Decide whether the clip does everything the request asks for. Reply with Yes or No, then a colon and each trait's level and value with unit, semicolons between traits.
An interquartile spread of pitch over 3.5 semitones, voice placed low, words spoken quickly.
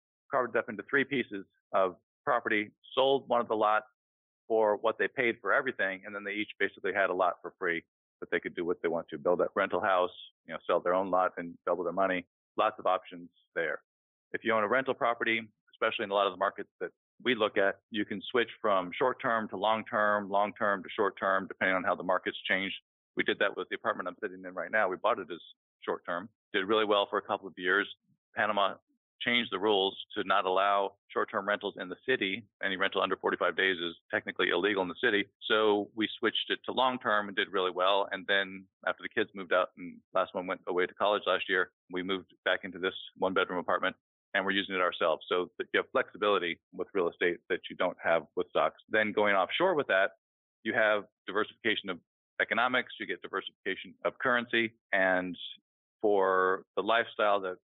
No: average, 2.8 semitones; low, 100 Hz; fast, 220 wpm